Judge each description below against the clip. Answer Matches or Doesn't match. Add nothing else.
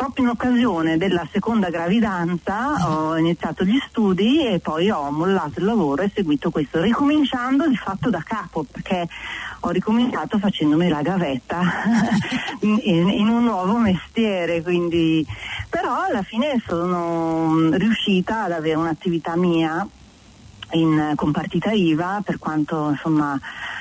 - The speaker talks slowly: Doesn't match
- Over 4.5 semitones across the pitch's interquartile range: Matches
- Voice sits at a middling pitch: Matches